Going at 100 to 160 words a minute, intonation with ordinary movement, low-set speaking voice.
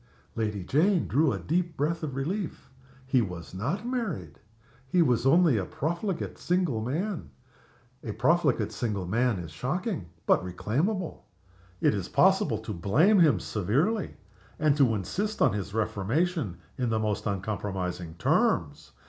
No: average, 140 wpm; wide, 8.9 semitones; low, 125 Hz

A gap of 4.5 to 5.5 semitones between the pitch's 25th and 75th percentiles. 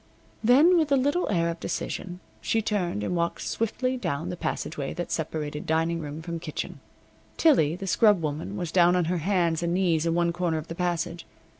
No: average, 3.4 semitones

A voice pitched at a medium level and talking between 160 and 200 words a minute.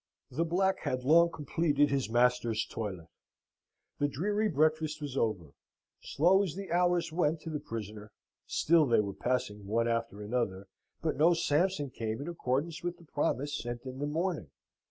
Yes: medium, 145 Hz; average, 165 wpm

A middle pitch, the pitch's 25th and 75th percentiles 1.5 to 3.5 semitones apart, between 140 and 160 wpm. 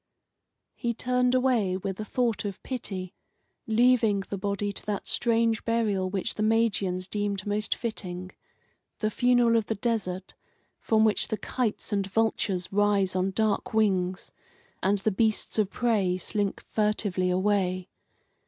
No: high, 205 Hz; average, 2.9 semitones; average, 145 wpm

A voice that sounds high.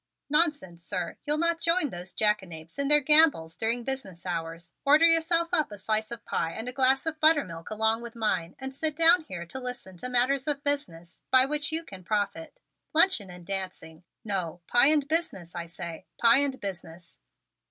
Yes: high, 235 Hz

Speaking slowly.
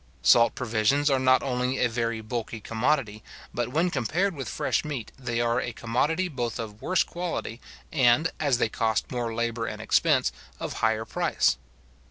No: average, 170 wpm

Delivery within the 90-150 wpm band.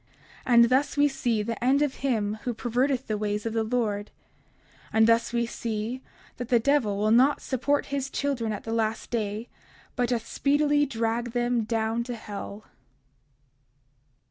No: average, 170 wpm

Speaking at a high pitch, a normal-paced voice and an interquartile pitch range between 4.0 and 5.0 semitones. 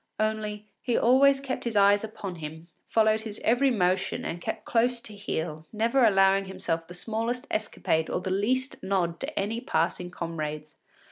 Yes: high, 205 Hz; average, 165 wpm; average, 4.5 semitones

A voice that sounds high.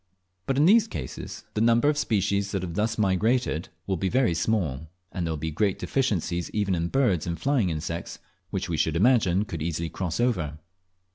No: very low, 95 Hz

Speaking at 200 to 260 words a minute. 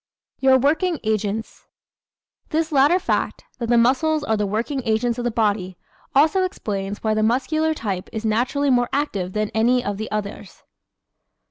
No: average, 165 wpm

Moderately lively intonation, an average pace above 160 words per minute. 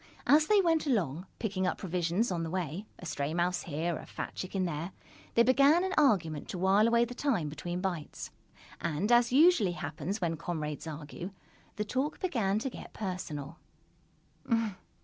No: wide, 6.3 semitones; average, 170 wpm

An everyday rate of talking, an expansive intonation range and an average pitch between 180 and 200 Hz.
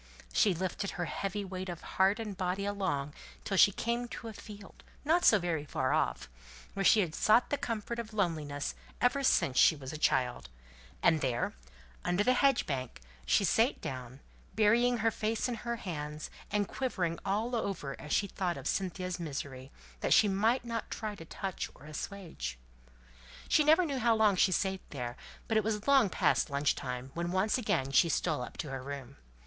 Yes: average, 190 wpm; wide, 6.7 semitones; high, 190 Hz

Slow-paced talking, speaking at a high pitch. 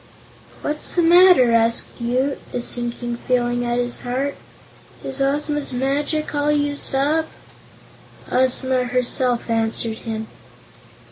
Yes: slow, 115 wpm; very high, 255 Hz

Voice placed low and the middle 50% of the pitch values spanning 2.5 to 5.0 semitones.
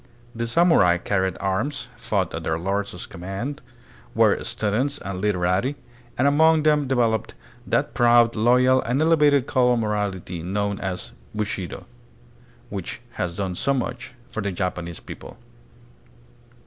No: low, 110 Hz; wide, 5.5 semitones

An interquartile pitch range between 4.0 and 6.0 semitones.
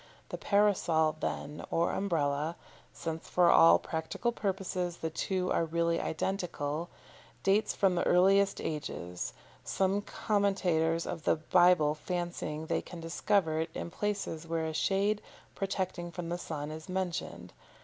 No: average, 3.3 semitones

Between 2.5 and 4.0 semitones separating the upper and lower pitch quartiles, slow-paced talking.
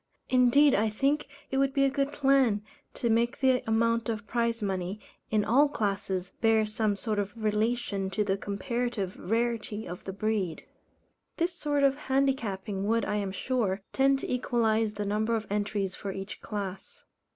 No: average, 3.7 semitones; average, 170 wpm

